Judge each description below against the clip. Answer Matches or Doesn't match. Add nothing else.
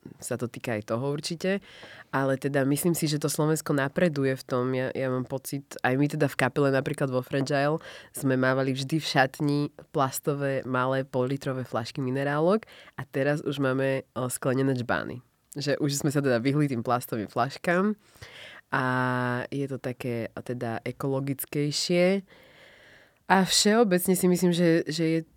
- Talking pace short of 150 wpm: Doesn't match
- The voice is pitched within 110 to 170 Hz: Matches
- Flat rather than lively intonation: Doesn't match